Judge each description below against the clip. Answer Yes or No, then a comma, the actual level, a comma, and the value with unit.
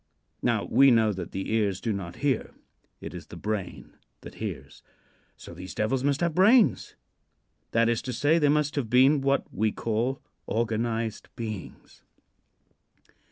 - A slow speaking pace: No, average, 155 wpm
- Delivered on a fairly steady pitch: No, average, 4.4 semitones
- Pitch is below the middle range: Yes, low, 115 Hz